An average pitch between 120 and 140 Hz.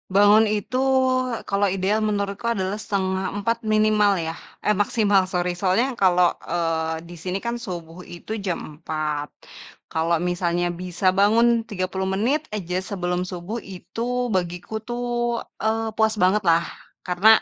No: high, 190 Hz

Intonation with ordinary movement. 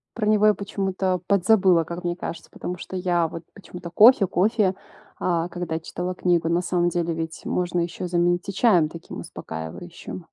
No: narrow, 2.1 semitones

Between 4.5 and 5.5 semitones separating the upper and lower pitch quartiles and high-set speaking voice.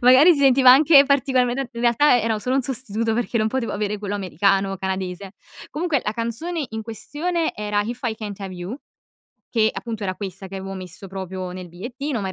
Yes: average, 5.1 semitones; high, 220 Hz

